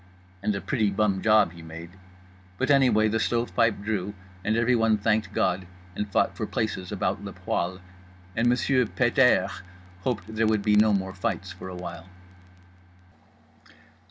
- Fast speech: No, average, 160 wpm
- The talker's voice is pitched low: Yes, low, 105 Hz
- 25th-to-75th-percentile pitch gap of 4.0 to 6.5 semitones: No, average, 3.2 semitones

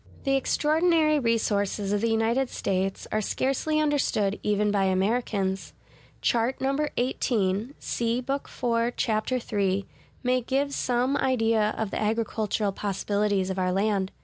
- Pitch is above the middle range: Yes, high, 225 Hz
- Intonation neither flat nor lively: Yes, average, 4.3 semitones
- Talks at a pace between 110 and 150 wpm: Yes, slow, 135 wpm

